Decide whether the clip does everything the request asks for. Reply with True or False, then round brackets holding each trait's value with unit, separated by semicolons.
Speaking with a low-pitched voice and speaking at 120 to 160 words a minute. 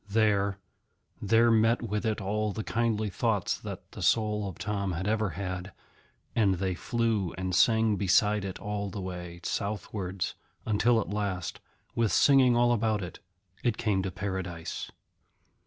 True (105 Hz; 155 wpm)